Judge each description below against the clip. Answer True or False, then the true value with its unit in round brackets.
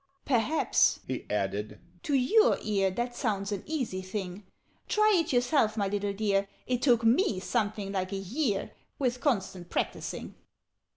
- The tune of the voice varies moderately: True (4.5 semitones)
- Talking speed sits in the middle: True (150 wpm)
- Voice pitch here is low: False (210 Hz)